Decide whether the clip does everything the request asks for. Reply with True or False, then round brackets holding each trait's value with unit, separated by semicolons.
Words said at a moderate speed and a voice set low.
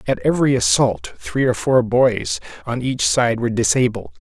True (170 wpm; 125 Hz)